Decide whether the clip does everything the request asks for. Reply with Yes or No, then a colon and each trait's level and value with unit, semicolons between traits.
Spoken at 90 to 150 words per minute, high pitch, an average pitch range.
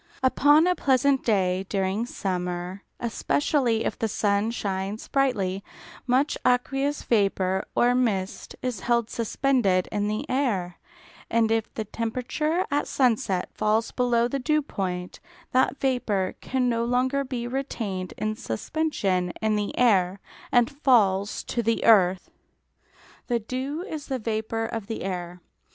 Yes: average, 140 wpm; high, 225 Hz; average, 4.8 semitones